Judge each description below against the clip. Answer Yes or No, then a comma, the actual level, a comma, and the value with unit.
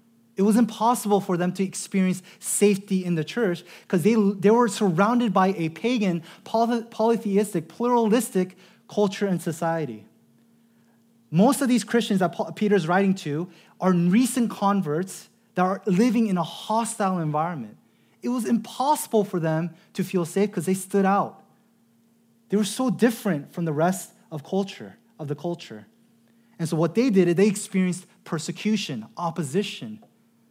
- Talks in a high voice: Yes, high, 200 Hz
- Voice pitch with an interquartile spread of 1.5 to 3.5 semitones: No, average, 4.2 semitones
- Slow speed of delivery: No, average, 150 wpm